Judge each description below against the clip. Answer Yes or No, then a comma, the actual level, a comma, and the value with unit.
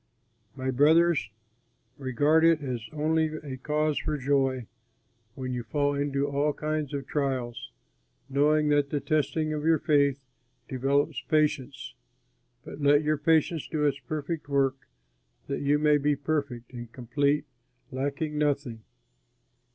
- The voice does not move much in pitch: Yes, narrow, 2.2 semitones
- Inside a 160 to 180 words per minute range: No, slow, 135 wpm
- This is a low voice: No, medium, 145 Hz